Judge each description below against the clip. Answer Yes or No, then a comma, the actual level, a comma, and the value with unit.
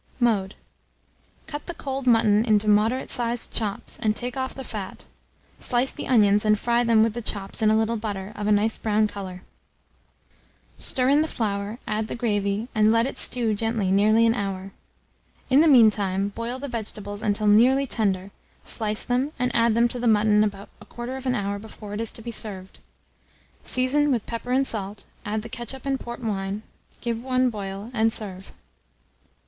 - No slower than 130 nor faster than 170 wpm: No, average, 185 wpm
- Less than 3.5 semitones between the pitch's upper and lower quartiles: Yes, average, 2.9 semitones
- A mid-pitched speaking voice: No, high, 220 Hz